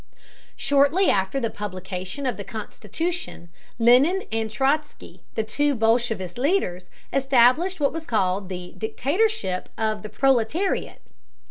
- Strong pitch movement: Yes, wide, 6.0 semitones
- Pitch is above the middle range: Yes, high, 240 Hz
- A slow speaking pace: Yes, slow, 120 wpm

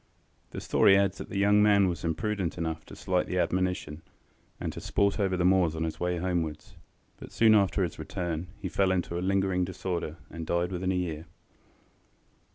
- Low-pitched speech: Yes, very low, 90 Hz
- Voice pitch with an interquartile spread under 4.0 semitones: Yes, narrow, 2.4 semitones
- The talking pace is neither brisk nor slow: Yes, average, 190 wpm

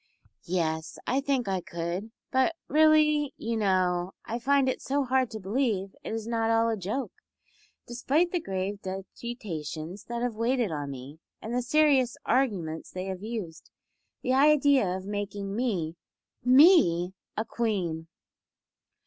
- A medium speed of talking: Yes, average, 145 wpm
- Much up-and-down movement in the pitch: Yes, wide, 5.9 semitones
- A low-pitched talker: No, high, 220 Hz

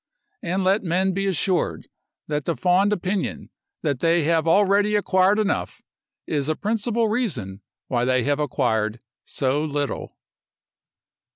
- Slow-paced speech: Yes, slow, 130 wpm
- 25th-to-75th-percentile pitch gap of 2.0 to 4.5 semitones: No, wide, 5.5 semitones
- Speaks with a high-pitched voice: No, medium, 170 Hz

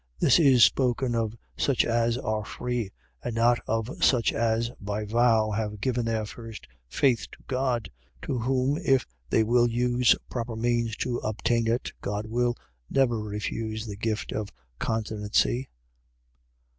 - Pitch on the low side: Yes, low, 115 Hz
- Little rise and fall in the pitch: Yes, narrow, 2.0 semitones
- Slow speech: No, average, 145 wpm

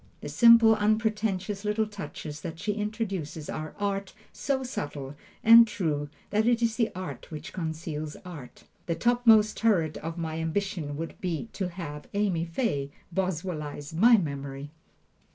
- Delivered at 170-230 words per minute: No, average, 145 wpm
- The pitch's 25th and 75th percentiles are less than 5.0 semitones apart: No, wide, 5.6 semitones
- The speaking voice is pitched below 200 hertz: Yes, medium, 185 Hz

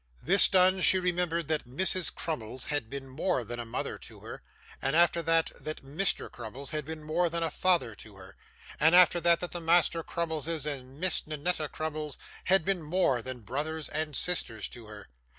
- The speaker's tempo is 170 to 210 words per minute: Yes, average, 190 wpm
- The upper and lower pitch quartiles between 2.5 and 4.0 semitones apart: No, average, 4.5 semitones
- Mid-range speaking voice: Yes, medium, 155 Hz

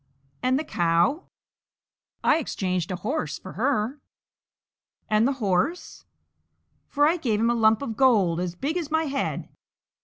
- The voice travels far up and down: Yes, wide, 7.4 semitones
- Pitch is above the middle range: Yes, high, 230 Hz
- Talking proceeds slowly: No, average, 150 wpm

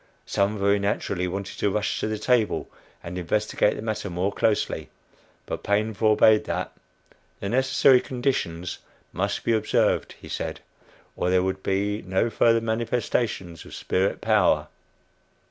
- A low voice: Yes, low, 105 Hz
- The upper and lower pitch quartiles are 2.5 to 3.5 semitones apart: Yes, average, 2.8 semitones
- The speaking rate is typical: Yes, average, 145 wpm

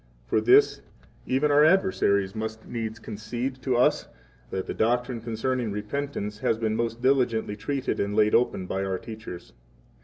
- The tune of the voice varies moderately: Yes, average, 3.6 semitones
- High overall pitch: No, low, 115 Hz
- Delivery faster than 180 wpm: No, average, 160 wpm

